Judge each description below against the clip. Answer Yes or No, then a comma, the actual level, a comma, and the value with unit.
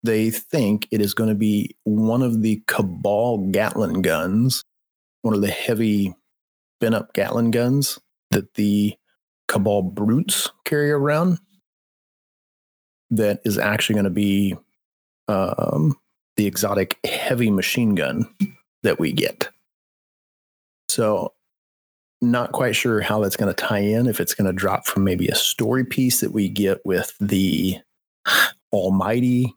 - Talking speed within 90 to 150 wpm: Yes, average, 140 wpm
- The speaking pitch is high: No, low, 105 Hz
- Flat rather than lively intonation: No, average, 3.3 semitones